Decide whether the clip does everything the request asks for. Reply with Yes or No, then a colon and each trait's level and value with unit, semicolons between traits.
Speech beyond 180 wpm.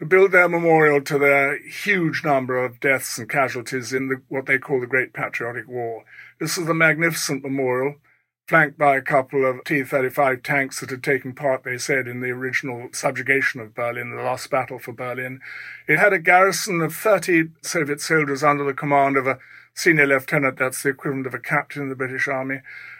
Yes: average, 200 wpm